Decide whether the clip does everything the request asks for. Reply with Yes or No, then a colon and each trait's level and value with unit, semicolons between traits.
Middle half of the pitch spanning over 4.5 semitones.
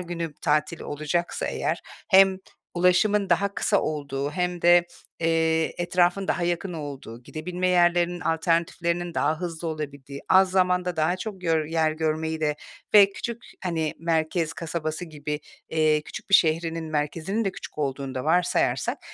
No: narrow, 2.5 semitones